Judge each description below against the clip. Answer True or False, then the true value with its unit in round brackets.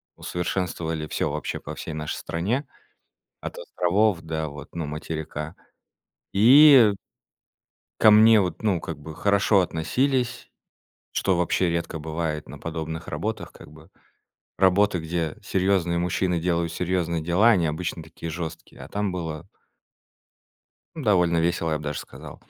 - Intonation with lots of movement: False (3.3 semitones)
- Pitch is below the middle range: True (85 Hz)